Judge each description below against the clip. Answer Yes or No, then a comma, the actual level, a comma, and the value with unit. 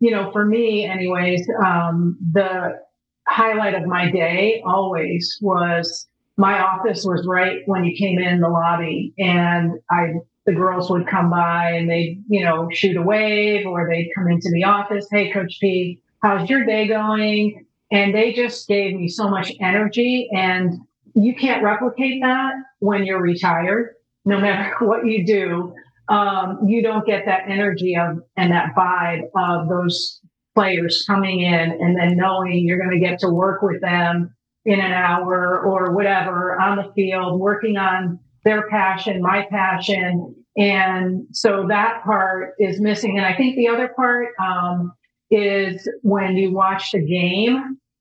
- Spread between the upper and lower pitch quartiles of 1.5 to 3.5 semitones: Yes, average, 2.8 semitones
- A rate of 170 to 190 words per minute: No, average, 160 wpm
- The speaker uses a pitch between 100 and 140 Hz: No, high, 190 Hz